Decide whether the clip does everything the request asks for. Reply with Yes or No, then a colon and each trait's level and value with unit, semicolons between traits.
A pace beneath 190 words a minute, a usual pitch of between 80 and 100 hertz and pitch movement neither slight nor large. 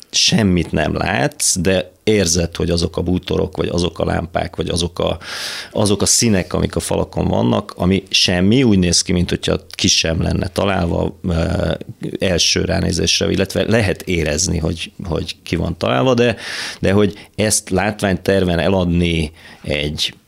No: average, 150 wpm; very low, 95 Hz; narrow, 2.3 semitones